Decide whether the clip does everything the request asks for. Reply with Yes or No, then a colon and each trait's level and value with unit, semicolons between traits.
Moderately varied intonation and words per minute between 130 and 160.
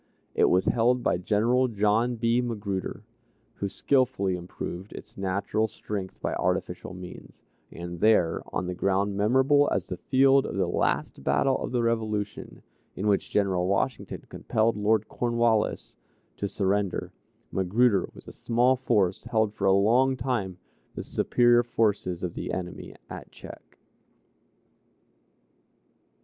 Yes: average, 4.0 semitones; slow, 135 wpm